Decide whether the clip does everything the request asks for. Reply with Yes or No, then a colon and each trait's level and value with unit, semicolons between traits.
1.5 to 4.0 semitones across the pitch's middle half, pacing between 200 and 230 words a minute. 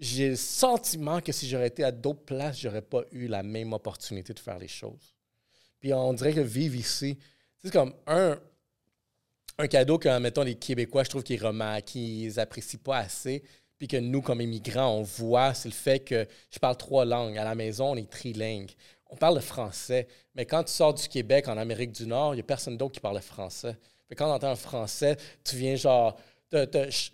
Yes: average, 3.5 semitones; fast, 220 wpm